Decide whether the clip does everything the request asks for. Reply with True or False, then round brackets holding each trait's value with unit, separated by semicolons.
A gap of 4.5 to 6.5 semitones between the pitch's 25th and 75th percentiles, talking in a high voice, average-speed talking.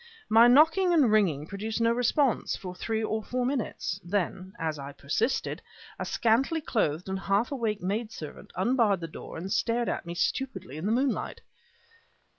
True (4.9 semitones; 215 Hz; 170 wpm)